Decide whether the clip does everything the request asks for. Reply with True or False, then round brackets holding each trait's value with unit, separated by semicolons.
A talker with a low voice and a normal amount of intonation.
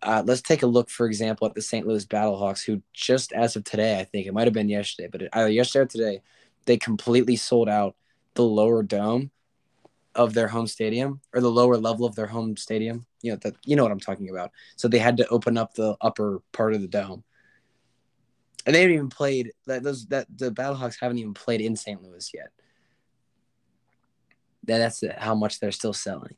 False (115 Hz; 2.2 semitones)